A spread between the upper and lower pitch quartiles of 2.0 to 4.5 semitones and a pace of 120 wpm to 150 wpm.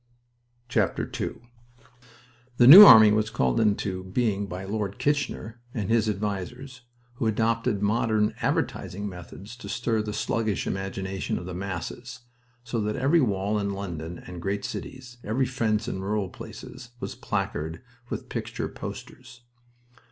Yes: average, 3.2 semitones; slow, 135 wpm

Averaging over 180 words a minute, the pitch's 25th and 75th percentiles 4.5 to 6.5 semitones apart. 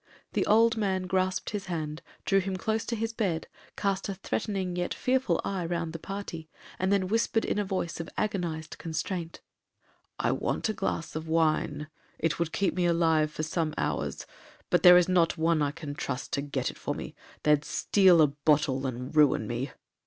No: average, 190 wpm; average, 3.9 semitones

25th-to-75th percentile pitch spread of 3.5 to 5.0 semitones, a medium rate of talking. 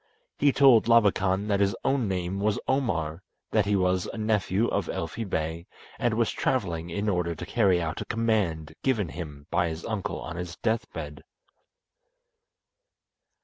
Yes: average, 4.7 semitones; average, 160 wpm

